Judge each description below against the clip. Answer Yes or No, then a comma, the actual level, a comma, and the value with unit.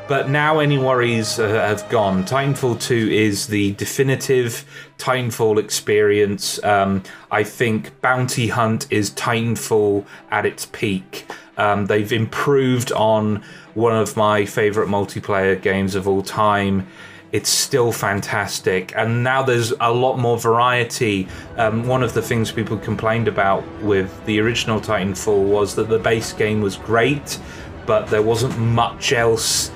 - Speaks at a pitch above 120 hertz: No, low, 110 Hz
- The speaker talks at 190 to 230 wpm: No, average, 145 wpm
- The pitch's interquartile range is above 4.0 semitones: No, average, 2.9 semitones